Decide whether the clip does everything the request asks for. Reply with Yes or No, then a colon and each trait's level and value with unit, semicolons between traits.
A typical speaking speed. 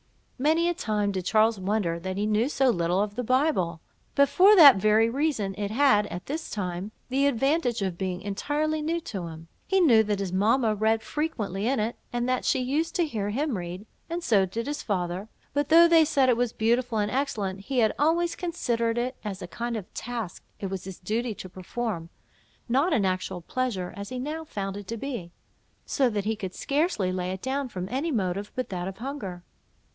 No: fast, 210 wpm